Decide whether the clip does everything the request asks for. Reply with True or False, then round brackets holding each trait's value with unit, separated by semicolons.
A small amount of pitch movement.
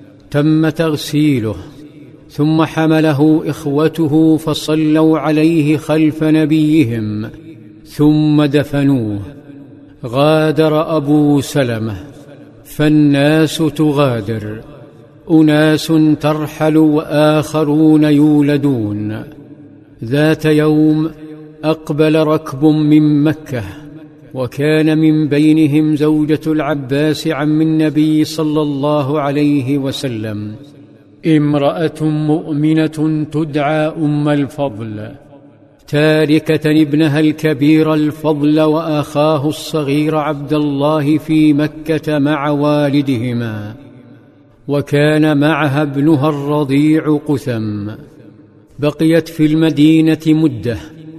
True (1.3 semitones)